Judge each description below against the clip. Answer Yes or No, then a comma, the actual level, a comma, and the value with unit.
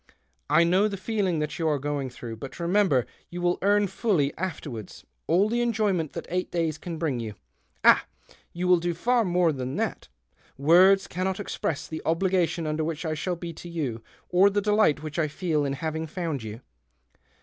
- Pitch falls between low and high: Yes, medium, 170 Hz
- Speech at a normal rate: Yes, average, 190 wpm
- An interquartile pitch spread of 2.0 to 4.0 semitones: Yes, average, 3.7 semitones